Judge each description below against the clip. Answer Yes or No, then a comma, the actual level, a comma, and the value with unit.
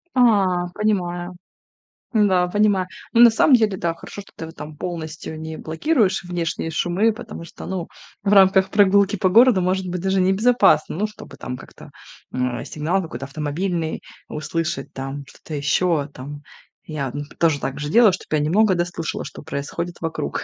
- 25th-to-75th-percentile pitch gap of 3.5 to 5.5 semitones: Yes, average, 4.1 semitones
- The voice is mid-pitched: Yes, medium, 175 Hz